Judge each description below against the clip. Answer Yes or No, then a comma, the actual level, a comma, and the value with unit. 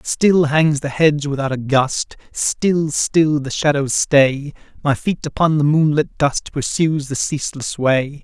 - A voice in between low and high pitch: Yes, medium, 145 Hz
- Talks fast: No, average, 160 wpm